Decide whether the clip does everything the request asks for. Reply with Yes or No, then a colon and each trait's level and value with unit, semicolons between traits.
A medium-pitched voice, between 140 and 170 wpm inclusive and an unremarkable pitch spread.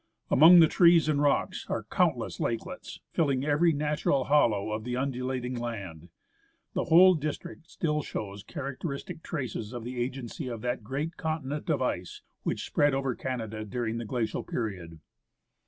No: low, 130 Hz; average, 155 wpm; average, 4.6 semitones